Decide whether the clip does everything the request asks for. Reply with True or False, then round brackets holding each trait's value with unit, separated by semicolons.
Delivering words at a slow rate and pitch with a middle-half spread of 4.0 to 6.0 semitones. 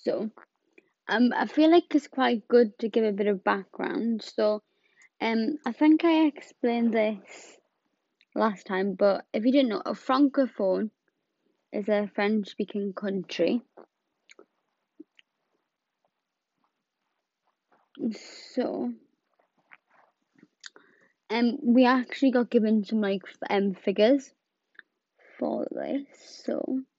True (105 wpm; 5.1 semitones)